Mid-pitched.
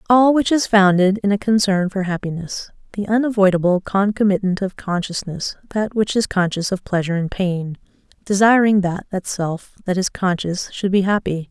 No: high, 195 Hz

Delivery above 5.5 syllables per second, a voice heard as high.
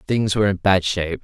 No: 6.5 syllables/s; very low, 95 Hz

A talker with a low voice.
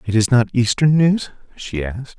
Yes: low, 125 Hz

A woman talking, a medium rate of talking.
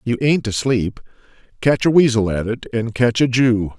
No: male; average, 190 wpm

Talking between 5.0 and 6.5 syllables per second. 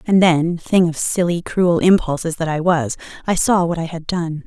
No: 4.7 syllables/s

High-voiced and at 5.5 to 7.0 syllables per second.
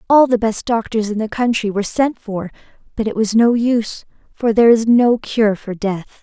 No: high, 220 Hz; 5.1 syllables/s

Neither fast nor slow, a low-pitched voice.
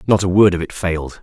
No: fast, 295 wpm; very low, 90 Hz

